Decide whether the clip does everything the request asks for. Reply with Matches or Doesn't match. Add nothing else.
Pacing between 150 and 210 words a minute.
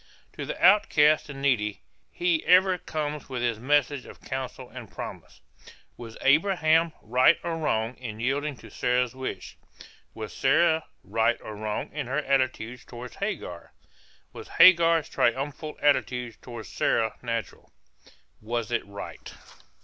Doesn't match